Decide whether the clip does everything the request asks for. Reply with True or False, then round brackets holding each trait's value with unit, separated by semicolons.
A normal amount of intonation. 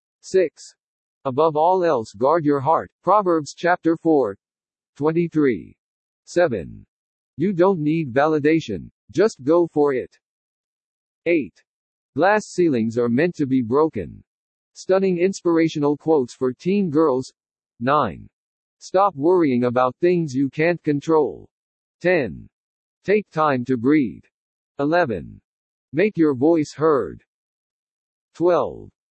True (3.6 semitones)